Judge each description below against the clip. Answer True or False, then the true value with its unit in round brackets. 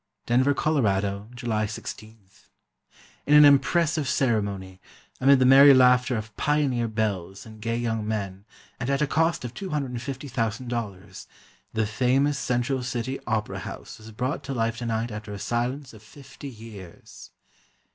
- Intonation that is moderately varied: True (3.9 semitones)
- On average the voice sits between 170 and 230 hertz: False (120 Hz)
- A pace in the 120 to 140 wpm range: True (135 wpm)